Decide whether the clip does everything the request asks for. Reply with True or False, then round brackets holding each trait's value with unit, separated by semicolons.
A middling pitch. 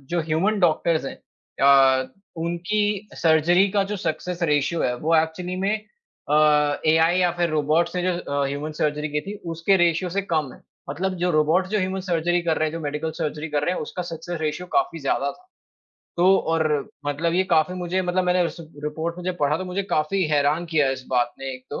True (165 Hz)